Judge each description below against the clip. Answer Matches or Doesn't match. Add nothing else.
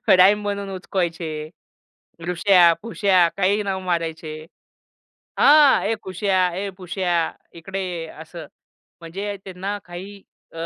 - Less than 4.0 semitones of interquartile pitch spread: Matches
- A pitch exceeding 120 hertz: Matches